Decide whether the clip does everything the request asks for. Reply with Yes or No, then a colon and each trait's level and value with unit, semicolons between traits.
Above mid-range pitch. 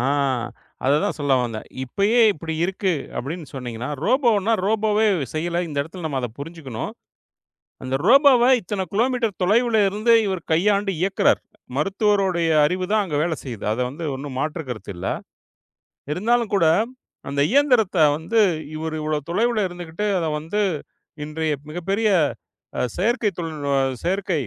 No: medium, 180 Hz